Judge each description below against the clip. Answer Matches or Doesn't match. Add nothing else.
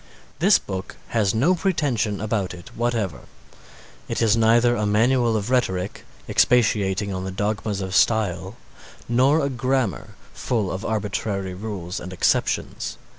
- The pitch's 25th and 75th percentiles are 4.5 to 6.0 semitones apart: Doesn't match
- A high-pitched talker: Doesn't match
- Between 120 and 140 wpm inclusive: Matches